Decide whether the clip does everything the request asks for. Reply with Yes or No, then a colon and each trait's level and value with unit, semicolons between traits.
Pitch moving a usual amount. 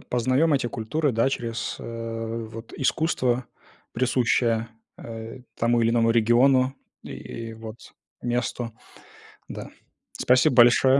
No: narrow, 2.0 semitones